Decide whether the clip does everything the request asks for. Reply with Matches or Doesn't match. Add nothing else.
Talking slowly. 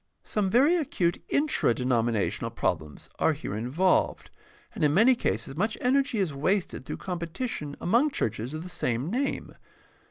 Doesn't match